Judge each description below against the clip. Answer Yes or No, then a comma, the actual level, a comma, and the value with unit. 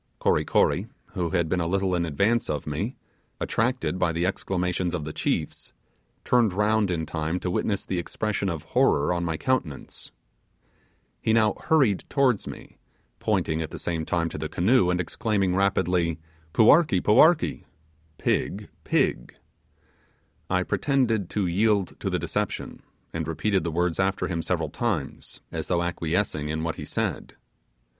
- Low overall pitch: Yes, very low, 90 Hz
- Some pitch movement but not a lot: Yes, average, 4.1 semitones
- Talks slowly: No, average, 155 wpm